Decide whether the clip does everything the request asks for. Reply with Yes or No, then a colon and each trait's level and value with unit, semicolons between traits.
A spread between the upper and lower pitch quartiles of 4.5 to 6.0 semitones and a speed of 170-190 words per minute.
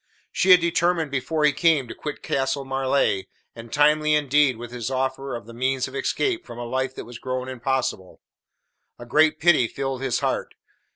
No: average, 3.1 semitones; average, 185 wpm